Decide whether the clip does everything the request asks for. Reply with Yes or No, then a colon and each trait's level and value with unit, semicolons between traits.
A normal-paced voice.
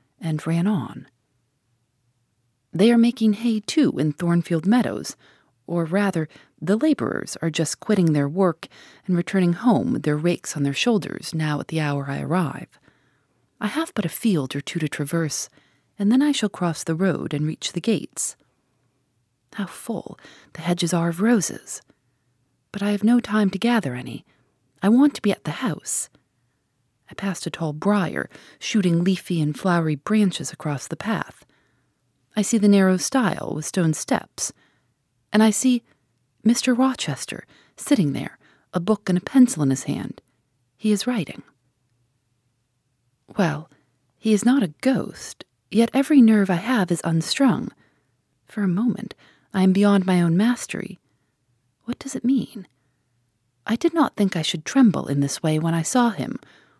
Yes: average, 165 wpm